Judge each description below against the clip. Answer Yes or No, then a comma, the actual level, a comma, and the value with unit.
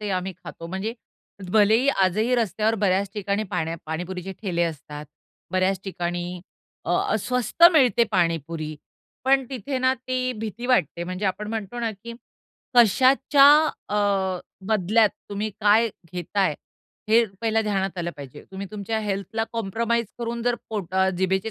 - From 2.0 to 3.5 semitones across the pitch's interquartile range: No, average, 4.0 semitones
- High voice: Yes, high, 205 Hz